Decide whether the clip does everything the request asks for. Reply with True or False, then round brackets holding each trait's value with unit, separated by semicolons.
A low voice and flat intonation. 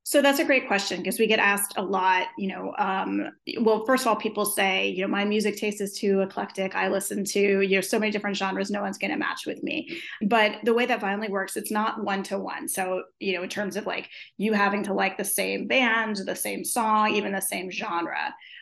False (205 Hz; 2.2 semitones)